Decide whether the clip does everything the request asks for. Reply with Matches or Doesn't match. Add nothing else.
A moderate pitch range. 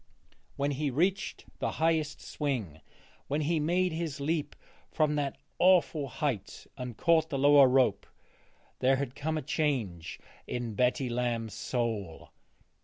Matches